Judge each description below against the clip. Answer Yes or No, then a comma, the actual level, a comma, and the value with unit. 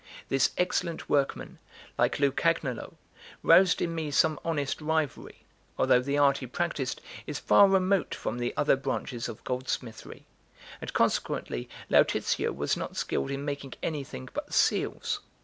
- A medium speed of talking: Yes, average, 145 wpm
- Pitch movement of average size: Yes, average, 4.3 semitones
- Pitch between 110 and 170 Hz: Yes, medium, 140 Hz